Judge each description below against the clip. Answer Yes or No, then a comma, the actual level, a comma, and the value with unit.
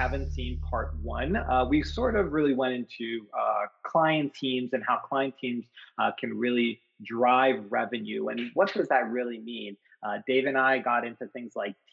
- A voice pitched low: Yes, low, 125 Hz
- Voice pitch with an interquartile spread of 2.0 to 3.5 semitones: Yes, average, 2.7 semitones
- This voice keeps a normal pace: Yes, average, 185 wpm